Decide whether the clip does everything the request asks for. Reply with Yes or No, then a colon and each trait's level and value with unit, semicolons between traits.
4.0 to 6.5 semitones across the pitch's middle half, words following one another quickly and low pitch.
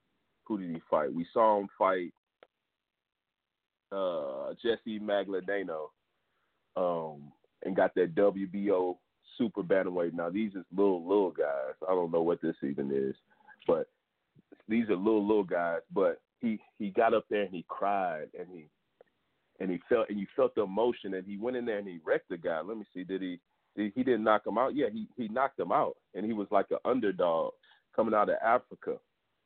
No: average, 5.2 semitones; average, 195 wpm; low, 100 Hz